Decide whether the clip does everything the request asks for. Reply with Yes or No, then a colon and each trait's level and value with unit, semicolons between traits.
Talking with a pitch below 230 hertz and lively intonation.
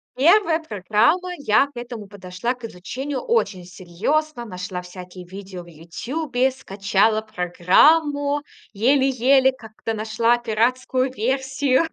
No: high, 235 Hz; wide, 5.9 semitones